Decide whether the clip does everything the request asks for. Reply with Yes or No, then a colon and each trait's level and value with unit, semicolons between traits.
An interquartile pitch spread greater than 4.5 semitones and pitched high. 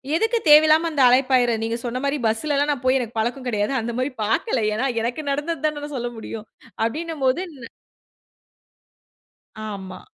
No: average, 4.2 semitones; very high, 255 Hz